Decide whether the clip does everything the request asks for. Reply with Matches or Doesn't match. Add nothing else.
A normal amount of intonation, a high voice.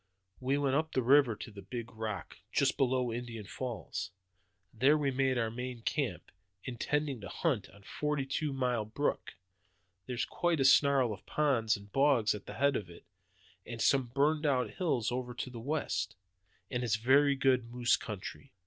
Doesn't match